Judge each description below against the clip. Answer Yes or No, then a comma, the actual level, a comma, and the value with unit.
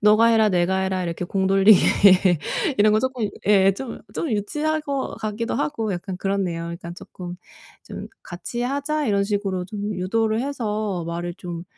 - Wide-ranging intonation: No, average, 3.8 semitones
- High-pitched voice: Yes, high, 205 Hz